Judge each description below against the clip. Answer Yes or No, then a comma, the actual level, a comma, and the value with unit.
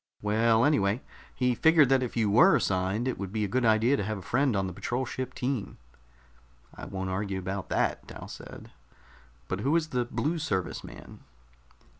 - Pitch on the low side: Yes, low, 115 Hz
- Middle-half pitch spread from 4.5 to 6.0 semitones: Yes, average, 4.8 semitones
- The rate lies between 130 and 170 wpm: No, average, 190 wpm